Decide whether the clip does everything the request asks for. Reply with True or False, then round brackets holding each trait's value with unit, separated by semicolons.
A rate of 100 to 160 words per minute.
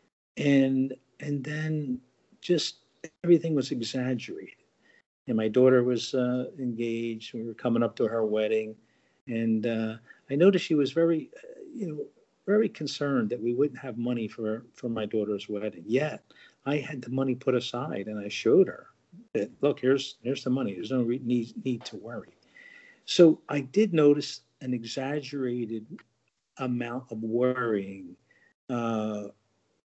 True (155 wpm)